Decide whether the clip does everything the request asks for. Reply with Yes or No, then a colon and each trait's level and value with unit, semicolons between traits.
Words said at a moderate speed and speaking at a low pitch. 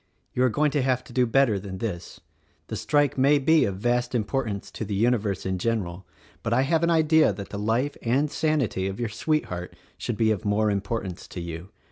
No: fast, 210 wpm; low, 115 Hz